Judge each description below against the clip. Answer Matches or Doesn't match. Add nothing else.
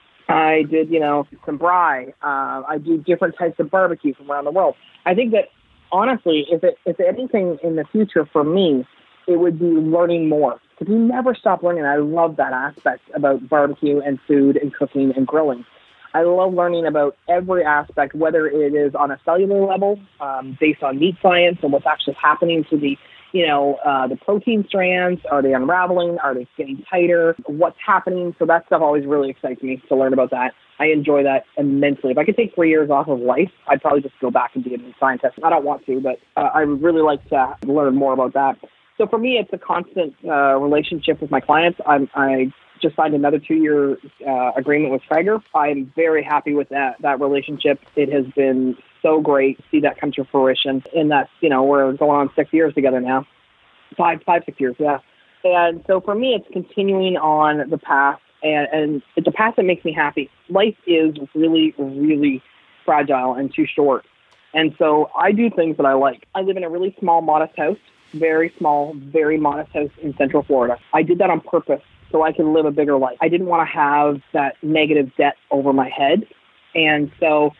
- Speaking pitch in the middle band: Matches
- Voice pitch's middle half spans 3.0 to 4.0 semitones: Matches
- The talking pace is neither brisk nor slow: Doesn't match